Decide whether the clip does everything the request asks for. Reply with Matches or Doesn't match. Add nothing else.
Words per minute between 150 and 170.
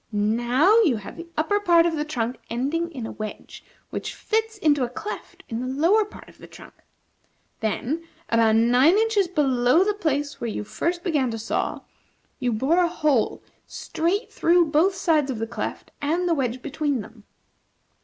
Doesn't match